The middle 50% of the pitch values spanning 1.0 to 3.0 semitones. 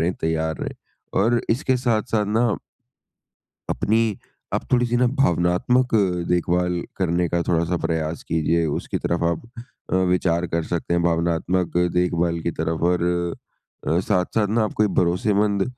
No: average, 4.2 semitones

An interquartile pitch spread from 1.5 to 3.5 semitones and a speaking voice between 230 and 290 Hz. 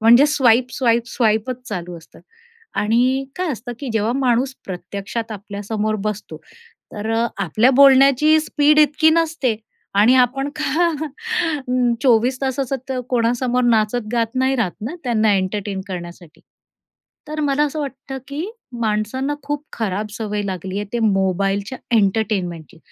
No: average, 4.6 semitones; high, 235 Hz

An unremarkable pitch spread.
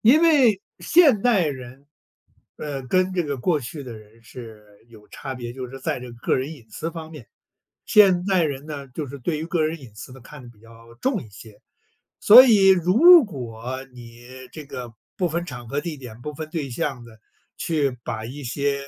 No: wide, 6.0 semitones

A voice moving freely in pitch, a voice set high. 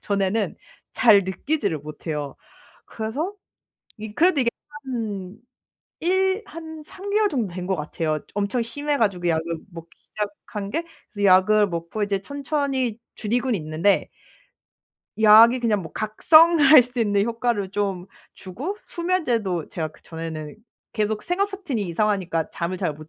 Yes: wide, 6.5 semitones; high, 210 Hz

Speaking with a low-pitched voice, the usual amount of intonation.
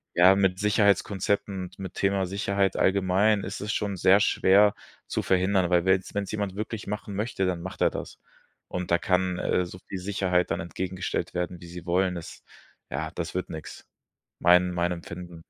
No: very low, 95 Hz; narrow, 1.9 semitones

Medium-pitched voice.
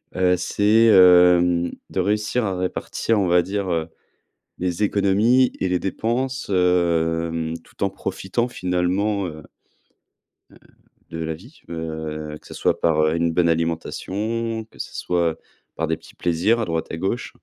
No: very low, 90 Hz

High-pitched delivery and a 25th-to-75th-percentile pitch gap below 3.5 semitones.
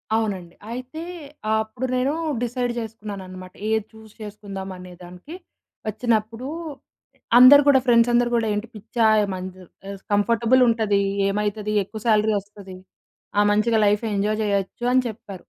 Yes: high, 215 Hz; average, 2.8 semitones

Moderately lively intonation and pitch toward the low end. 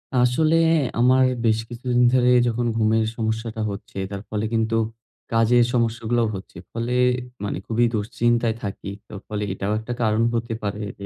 No: narrow, 1.7 semitones; low, 115 Hz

